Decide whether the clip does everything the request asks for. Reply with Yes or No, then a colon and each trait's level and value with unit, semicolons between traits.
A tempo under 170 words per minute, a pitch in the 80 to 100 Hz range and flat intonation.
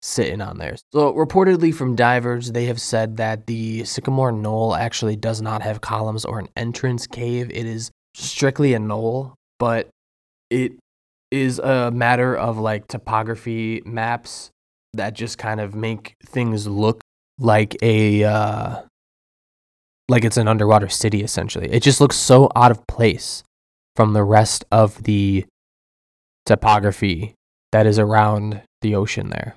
No: average, 145 wpm; low, 110 Hz; narrow, 2.3 semitones